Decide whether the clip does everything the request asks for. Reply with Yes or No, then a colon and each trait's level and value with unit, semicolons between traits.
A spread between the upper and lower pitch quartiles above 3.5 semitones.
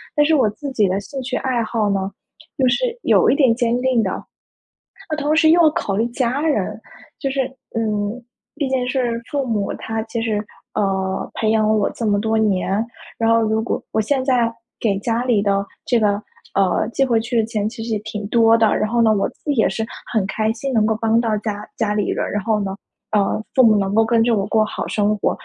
No: average, 3.0 semitones